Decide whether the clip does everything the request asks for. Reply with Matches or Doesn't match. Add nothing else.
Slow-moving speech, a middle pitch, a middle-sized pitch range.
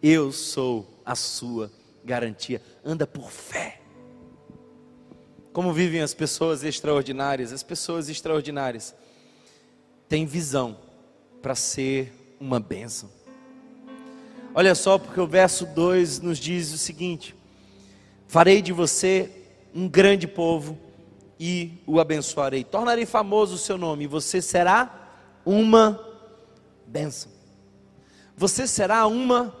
Doesn't match